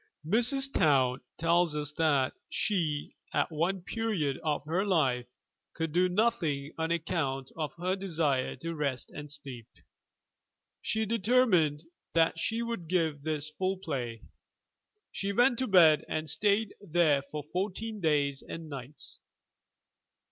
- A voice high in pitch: No, medium, 160 Hz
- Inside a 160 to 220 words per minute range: No, slow, 135 wpm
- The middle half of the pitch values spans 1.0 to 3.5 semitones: No, average, 4.8 semitones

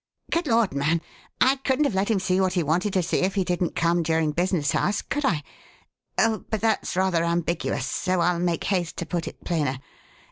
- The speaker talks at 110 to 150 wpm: No, fast, 205 wpm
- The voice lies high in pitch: No, medium, 180 Hz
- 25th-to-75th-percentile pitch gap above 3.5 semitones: No, average, 3.2 semitones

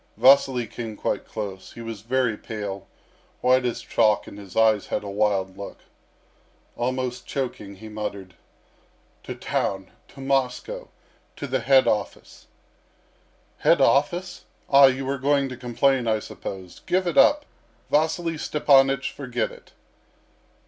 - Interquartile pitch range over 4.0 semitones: Yes, average, 4.4 semitones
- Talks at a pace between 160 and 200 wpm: No, slow, 135 wpm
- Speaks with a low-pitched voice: Yes, low, 125 Hz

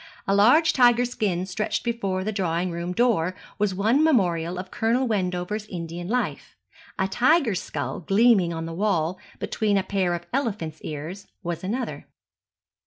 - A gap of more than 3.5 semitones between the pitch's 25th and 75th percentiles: Yes, average, 4.6 semitones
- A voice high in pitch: Yes, high, 195 Hz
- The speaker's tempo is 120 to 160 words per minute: Yes, average, 155 wpm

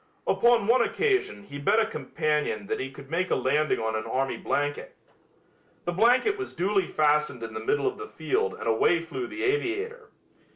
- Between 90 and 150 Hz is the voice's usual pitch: No, high, 190 Hz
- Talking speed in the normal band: Yes, average, 190 wpm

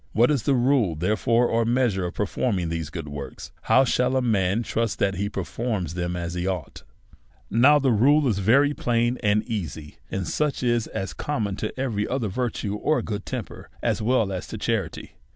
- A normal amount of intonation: Yes, average, 4.8 semitones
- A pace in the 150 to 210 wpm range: Yes, average, 190 wpm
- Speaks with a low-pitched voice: Yes, low, 110 Hz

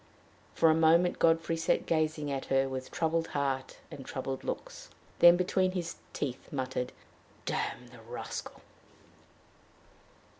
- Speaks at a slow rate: Yes, slow, 125 wpm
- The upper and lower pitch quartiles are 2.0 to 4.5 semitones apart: Yes, average, 3.8 semitones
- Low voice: No, medium, 150 Hz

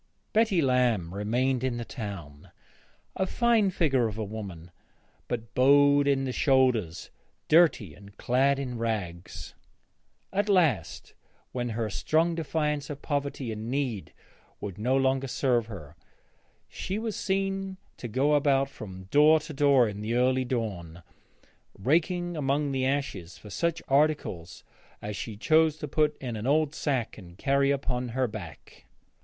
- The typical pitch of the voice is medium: No, low, 130 Hz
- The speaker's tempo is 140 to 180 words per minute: Yes, average, 150 wpm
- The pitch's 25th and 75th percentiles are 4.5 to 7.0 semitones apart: Yes, wide, 5.5 semitones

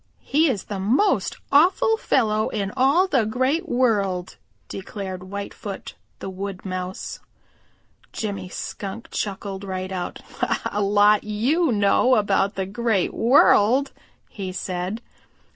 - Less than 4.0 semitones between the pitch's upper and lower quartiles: No, average, 4.7 semitones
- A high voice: Yes, high, 205 Hz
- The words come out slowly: Yes, slow, 120 wpm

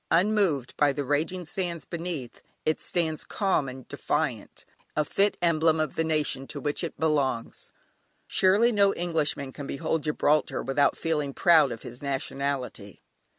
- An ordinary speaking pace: Yes, average, 150 wpm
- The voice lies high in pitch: No, medium, 155 Hz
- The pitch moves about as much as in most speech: Yes, average, 3.4 semitones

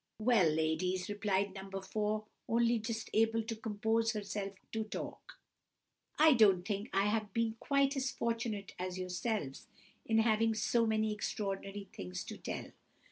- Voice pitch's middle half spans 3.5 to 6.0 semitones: No, narrow, 2.6 semitones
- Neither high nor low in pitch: No, high, 215 Hz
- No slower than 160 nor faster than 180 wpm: No, average, 145 wpm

